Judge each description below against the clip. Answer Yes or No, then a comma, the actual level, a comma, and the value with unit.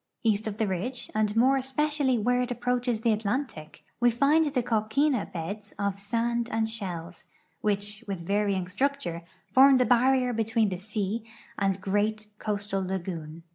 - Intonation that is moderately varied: Yes, average, 3.7 semitones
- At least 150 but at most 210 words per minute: Yes, average, 160 wpm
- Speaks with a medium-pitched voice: No, high, 215 Hz